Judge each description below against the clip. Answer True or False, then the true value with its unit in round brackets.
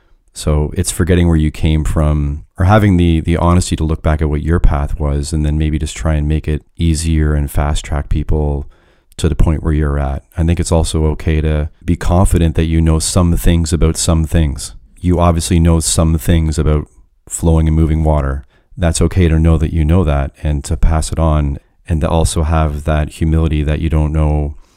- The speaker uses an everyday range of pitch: False (1.8 semitones)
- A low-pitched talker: True (80 Hz)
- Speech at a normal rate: False (215 wpm)